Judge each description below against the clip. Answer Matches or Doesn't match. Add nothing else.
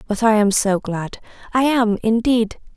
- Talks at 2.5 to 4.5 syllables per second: Matches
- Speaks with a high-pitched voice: Matches